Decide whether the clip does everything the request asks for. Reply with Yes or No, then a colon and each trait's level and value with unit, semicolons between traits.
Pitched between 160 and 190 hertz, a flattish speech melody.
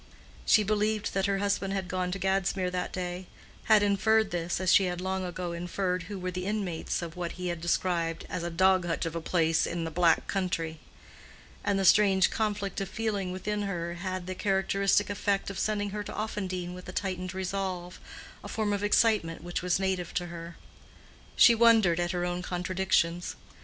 Yes: medium, 185 Hz; narrow, 2.1 semitones